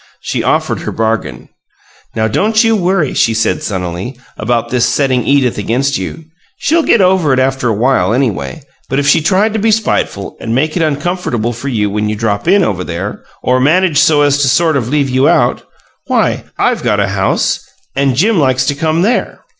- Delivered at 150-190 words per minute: No, average, 200 wpm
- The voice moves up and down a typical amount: No, wide, 6.5 semitones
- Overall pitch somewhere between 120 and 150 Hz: Yes, low, 135 Hz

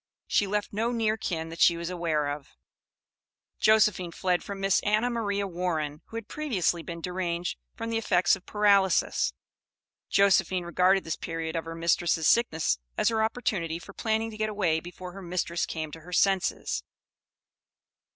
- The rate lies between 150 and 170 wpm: Yes, average, 165 wpm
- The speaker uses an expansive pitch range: No, average, 3.8 semitones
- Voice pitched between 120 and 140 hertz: No, medium, 180 Hz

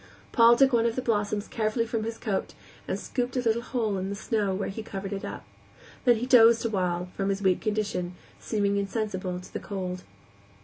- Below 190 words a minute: No, fast, 205 wpm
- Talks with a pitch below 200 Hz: No, high, 215 Hz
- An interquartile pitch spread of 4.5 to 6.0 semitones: No, average, 2.9 semitones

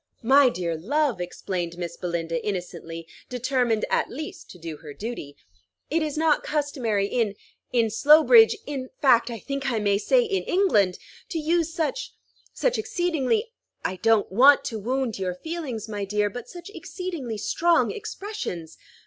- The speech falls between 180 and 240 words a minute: No, average, 155 wpm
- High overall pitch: Yes, high, 245 Hz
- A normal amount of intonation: No, wide, 7.9 semitones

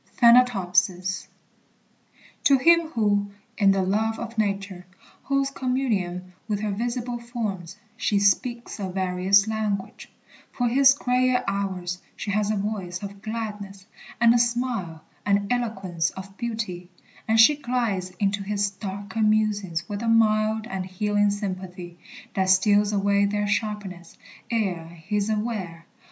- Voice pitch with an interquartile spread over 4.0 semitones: No, average, 3.0 semitones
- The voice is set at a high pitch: Yes, high, 205 Hz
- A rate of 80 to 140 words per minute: Yes, slow, 135 wpm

